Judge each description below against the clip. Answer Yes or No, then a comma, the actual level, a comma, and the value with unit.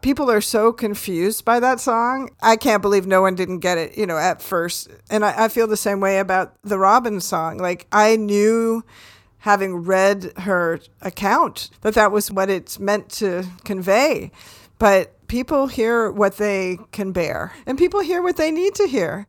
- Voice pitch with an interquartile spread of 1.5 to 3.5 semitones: Yes, average, 3.2 semitones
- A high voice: Yes, high, 205 Hz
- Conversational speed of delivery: Yes, average, 185 wpm